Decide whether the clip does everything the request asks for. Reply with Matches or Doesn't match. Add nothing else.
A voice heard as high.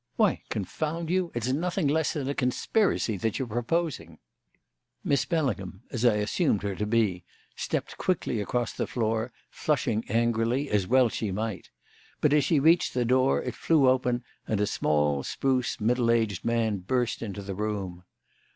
Doesn't match